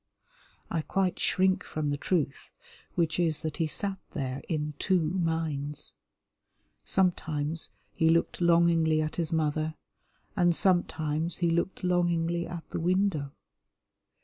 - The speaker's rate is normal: No, slow, 125 wpm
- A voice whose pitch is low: No, medium, 165 Hz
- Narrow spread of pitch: Yes, narrow, 2.2 semitones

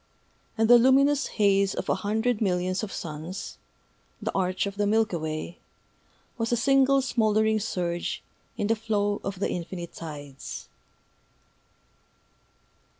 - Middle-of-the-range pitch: No, high, 205 Hz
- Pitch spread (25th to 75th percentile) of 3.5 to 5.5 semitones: Yes, average, 3.8 semitones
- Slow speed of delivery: Yes, slow, 130 wpm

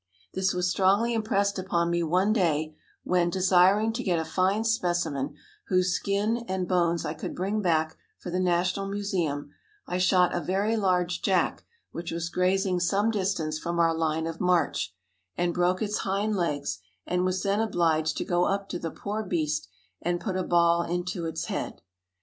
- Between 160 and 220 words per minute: Yes, average, 180 wpm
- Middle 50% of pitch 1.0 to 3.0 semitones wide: Yes, narrow, 2.5 semitones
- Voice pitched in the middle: Yes, medium, 180 Hz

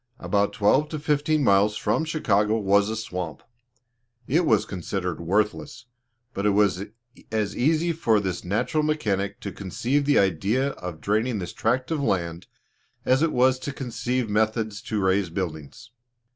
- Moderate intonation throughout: Yes, average, 4.9 semitones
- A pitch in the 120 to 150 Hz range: No, low, 105 Hz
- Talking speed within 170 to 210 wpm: No, average, 155 wpm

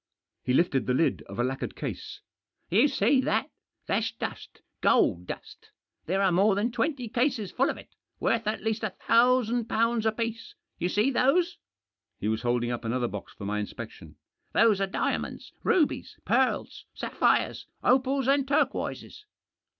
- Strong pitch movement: Yes, wide, 7.0 semitones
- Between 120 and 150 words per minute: No, average, 165 wpm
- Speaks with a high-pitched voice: Yes, high, 225 Hz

